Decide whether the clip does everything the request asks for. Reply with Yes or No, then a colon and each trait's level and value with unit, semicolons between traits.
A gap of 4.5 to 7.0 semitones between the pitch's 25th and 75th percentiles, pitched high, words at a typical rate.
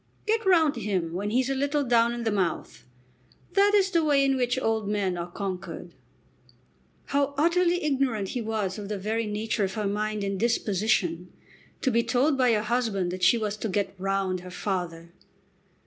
Yes: average, 5.2 semitones; high, 220 Hz; average, 185 wpm